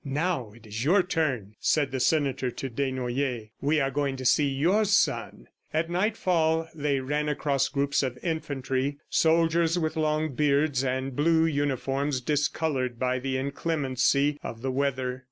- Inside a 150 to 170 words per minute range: Yes, average, 155 wpm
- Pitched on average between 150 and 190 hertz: No, medium, 140 Hz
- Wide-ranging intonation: No, average, 3.2 semitones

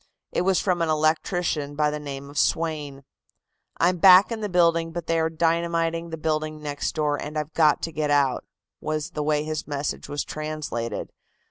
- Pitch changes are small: Yes, narrow, 2.0 semitones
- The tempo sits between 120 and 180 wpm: No, average, 190 wpm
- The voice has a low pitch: No, medium, 155 Hz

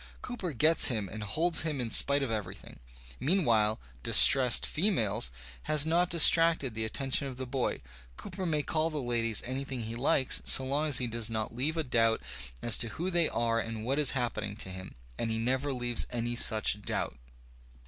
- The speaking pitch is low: Yes, low, 125 Hz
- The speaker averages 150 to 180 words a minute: No, average, 195 wpm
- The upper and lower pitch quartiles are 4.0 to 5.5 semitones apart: Yes, average, 4.9 semitones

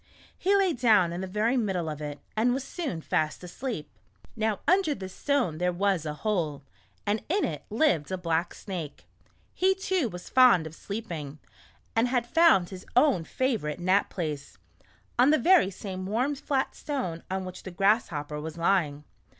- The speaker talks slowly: No, average, 175 wpm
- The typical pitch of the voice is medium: No, high, 195 Hz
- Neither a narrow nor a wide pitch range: No, wide, 7.2 semitones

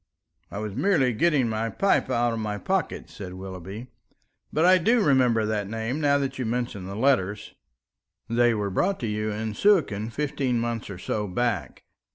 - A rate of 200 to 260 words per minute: No, average, 180 wpm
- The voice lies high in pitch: No, low, 115 Hz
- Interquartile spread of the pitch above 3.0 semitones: Yes, average, 4.6 semitones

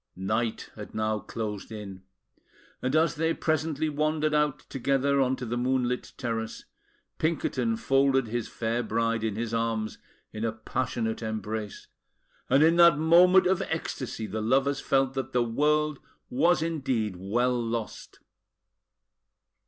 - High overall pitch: No, low, 125 Hz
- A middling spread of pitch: Yes, average, 5.0 semitones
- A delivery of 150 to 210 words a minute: No, slow, 135 wpm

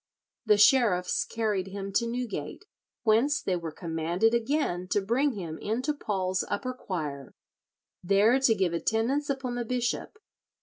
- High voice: Yes, high, 215 Hz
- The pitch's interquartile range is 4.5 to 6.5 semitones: Yes, average, 5.3 semitones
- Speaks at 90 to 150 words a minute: Yes, average, 140 wpm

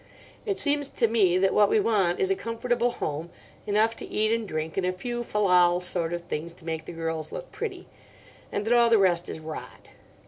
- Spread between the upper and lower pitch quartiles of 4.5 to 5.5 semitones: Yes, average, 5.1 semitones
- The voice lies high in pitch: Yes, high, 195 Hz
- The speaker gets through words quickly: Yes, fast, 220 wpm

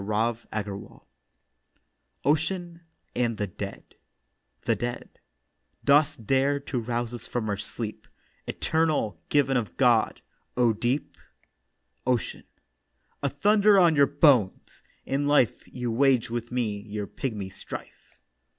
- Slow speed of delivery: Yes, slow, 115 wpm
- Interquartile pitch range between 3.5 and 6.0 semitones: Yes, average, 4.7 semitones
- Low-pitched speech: Yes, low, 120 Hz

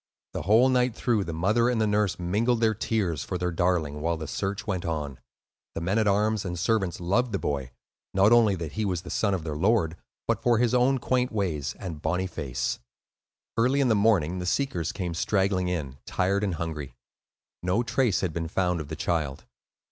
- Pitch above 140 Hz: No, very low, 95 Hz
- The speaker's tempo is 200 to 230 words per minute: Yes, fast, 205 wpm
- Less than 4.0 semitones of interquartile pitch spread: No, average, 4.8 semitones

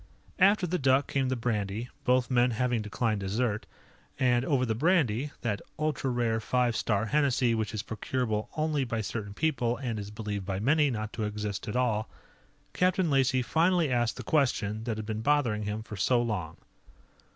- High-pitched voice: No, low, 120 Hz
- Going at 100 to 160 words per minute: No, average, 180 wpm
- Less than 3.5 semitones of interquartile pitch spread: No, average, 3.8 semitones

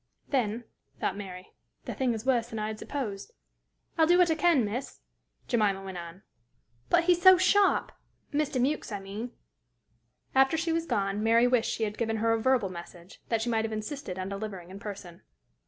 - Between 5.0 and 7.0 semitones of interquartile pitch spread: Yes, average, 5.3 semitones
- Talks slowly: No, average, 190 wpm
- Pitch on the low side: No, high, 225 Hz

